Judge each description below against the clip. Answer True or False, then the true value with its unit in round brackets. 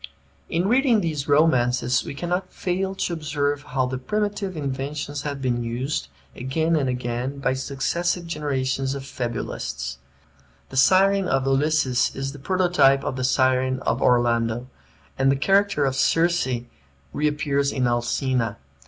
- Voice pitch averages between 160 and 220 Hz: False (140 Hz)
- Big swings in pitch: False (4.2 semitones)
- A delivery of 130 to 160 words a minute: True (140 wpm)